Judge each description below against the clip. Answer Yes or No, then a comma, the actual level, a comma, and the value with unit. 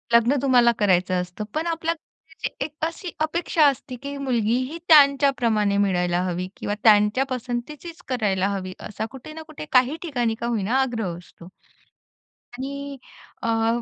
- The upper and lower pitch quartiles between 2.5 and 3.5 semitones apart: No, wide, 5.5 semitones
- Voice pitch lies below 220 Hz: No, high, 245 Hz